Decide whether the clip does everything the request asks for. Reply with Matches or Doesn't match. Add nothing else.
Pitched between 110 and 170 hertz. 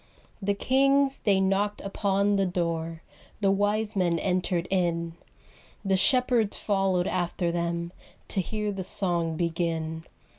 Doesn't match